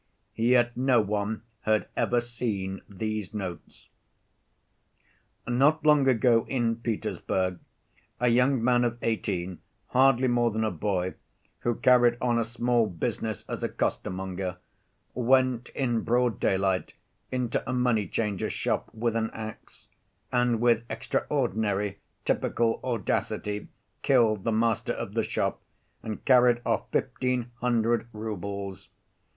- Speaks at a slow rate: Yes, slow, 125 wpm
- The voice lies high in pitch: No, low, 115 Hz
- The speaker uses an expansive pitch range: No, average, 2.9 semitones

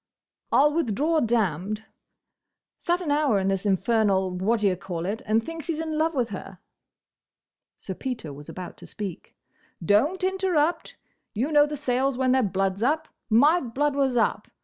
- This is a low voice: No, high, 240 Hz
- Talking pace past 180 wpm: No, average, 170 wpm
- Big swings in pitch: Yes, wide, 7.3 semitones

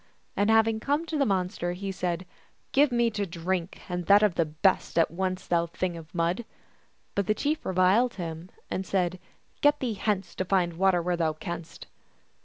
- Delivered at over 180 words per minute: Yes, fast, 205 wpm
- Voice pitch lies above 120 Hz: Yes, medium, 185 Hz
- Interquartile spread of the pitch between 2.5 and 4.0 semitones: Yes, average, 3.5 semitones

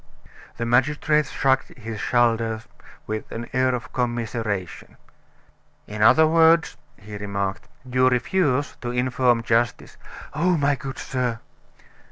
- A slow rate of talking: Yes, slow, 125 wpm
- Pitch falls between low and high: No, low, 125 Hz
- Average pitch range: Yes, average, 3.1 semitones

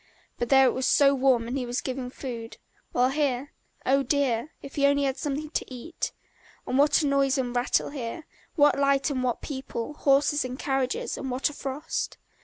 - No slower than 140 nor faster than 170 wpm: No, average, 200 wpm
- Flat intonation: Yes, narrow, 2.0 semitones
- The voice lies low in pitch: No, very high, 270 Hz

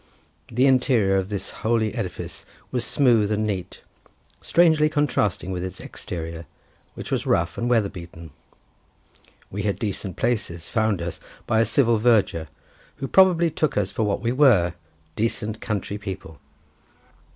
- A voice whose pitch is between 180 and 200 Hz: No, low, 105 Hz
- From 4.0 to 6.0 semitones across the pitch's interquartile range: Yes, average, 4.9 semitones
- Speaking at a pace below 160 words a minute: Yes, average, 140 wpm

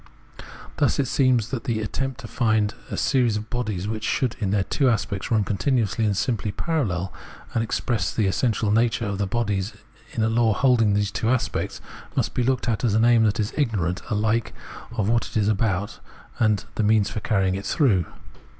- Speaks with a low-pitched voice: Yes, low, 110 Hz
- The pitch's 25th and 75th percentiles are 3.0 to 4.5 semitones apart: No, narrow, 2.6 semitones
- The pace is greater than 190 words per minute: Yes, average, 200 wpm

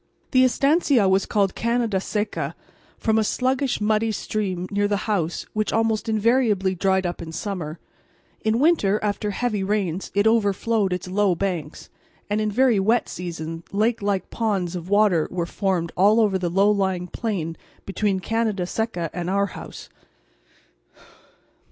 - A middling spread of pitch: Yes, average, 3.2 semitones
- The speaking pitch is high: Yes, high, 200 Hz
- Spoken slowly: No, average, 150 wpm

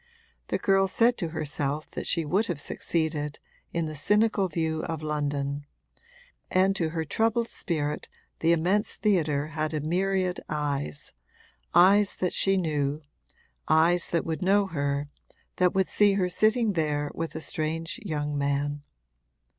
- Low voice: No, medium, 160 Hz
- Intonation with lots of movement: No, average, 4.3 semitones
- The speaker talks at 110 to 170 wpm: Yes, average, 145 wpm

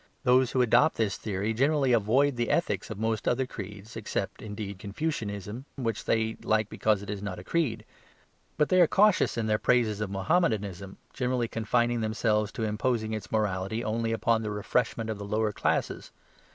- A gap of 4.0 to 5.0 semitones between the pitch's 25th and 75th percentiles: No, average, 2.9 semitones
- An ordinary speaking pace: Yes, average, 180 wpm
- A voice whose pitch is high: No, low, 110 Hz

